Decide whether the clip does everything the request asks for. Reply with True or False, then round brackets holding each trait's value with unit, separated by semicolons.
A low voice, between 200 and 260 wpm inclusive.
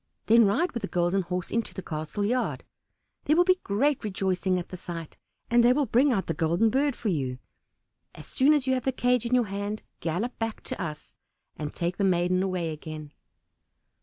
False (200 Hz; 205 wpm)